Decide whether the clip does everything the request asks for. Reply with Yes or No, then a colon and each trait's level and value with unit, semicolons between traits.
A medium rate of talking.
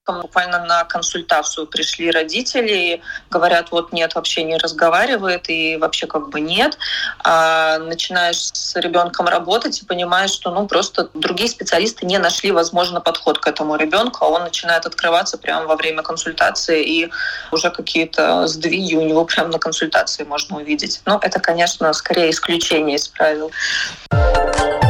Yes: average, 145 wpm